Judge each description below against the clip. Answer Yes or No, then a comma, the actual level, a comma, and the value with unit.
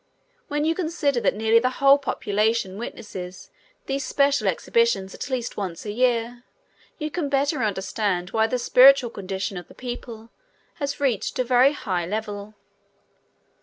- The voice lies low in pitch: No, high, 240 Hz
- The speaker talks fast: No, average, 155 wpm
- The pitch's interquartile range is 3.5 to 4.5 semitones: No, average, 5.1 semitones